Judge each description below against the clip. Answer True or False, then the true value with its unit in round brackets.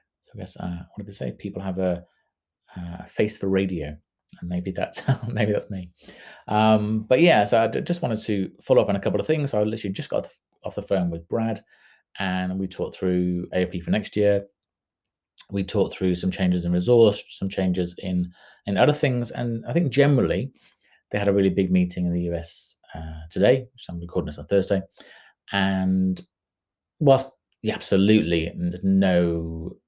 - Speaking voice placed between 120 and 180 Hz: False (95 Hz)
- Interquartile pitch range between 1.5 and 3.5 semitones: True (2.9 semitones)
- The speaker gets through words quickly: False (185 wpm)